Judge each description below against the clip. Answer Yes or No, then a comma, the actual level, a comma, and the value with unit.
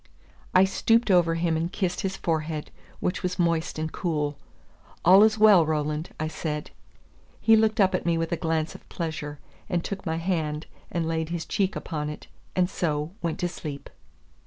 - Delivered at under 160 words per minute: No, average, 185 wpm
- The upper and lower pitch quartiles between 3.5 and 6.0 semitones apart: No, average, 2.8 semitones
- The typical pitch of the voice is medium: Yes, medium, 165 Hz